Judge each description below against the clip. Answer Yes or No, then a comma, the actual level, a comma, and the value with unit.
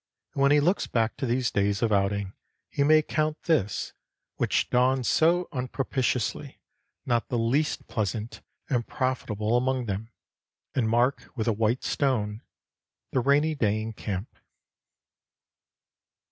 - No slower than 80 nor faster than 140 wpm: Yes, slow, 135 wpm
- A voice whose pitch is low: Yes, low, 120 Hz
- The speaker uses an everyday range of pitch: Yes, average, 4.1 semitones